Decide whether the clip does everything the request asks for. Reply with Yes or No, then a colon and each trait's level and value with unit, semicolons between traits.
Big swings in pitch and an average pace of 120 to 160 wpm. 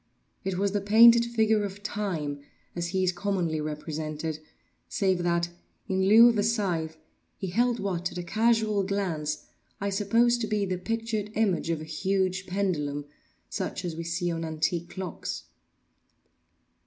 No: average, 3.7 semitones; average, 155 wpm